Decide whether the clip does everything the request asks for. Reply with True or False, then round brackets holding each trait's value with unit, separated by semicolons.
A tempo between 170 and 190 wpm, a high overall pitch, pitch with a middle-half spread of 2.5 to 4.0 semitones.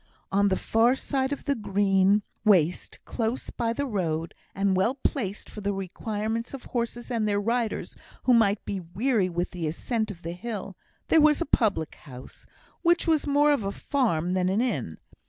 False (185 wpm; 210 Hz; 4.6 semitones)